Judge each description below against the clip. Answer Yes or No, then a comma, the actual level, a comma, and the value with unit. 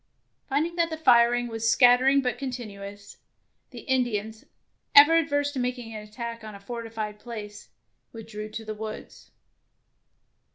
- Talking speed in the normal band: Yes, average, 150 wpm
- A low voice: No, high, 235 Hz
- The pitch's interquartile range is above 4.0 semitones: No, average, 3.3 semitones